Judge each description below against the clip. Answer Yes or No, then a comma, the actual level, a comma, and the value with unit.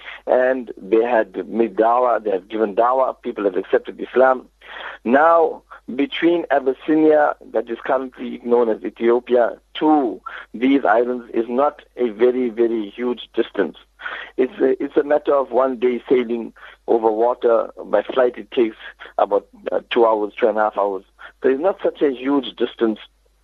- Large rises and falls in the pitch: No, average, 4.3 semitones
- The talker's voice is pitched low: Yes, low, 125 Hz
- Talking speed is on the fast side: No, average, 160 wpm